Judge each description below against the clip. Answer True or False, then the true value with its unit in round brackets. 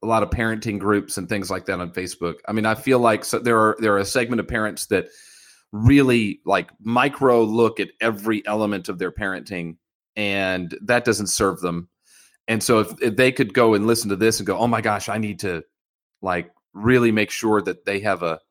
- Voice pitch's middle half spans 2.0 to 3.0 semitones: True (2.5 semitones)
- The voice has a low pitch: True (110 Hz)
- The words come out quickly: True (220 wpm)